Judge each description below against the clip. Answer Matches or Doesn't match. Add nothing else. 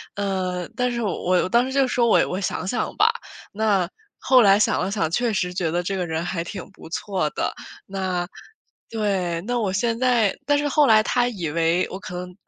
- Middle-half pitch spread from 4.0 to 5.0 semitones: Matches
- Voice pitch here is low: Doesn't match